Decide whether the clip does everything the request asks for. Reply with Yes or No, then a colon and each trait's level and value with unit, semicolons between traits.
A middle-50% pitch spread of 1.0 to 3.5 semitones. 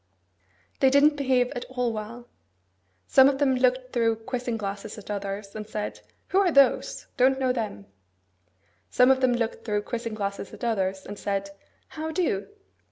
No: average, 4.0 semitones